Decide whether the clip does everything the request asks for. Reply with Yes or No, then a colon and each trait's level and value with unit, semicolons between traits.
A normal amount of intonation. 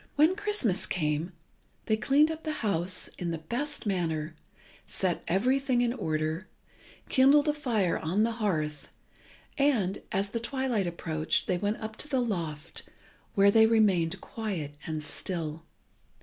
No: wide, 7.0 semitones